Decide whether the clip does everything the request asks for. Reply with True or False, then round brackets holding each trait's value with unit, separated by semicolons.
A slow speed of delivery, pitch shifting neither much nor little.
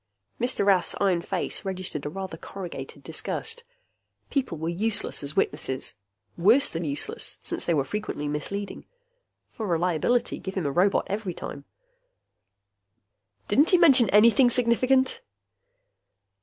False (130 wpm; 6.0 semitones)